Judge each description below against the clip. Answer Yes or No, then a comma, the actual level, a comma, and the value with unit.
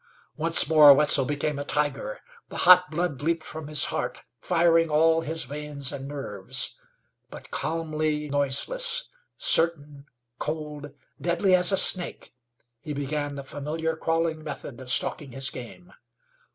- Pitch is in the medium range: Yes, medium, 150 Hz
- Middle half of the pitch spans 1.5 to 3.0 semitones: Yes, narrow, 2.6 semitones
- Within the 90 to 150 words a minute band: Yes, average, 140 wpm